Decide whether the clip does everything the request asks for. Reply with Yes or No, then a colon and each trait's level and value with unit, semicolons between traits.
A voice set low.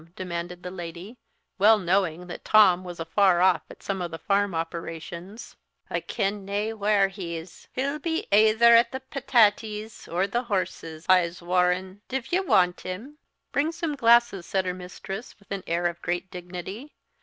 No: high, 190 Hz